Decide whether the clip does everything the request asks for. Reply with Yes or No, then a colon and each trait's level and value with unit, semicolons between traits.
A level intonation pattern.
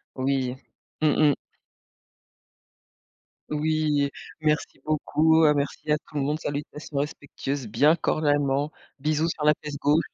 Yes: narrow, 1.5 semitones